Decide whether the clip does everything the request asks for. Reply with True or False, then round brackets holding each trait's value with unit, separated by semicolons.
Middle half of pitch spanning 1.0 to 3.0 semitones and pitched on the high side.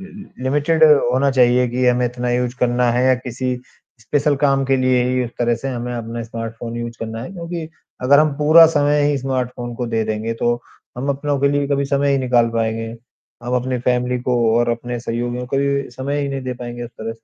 False (2.7 semitones; 125 Hz)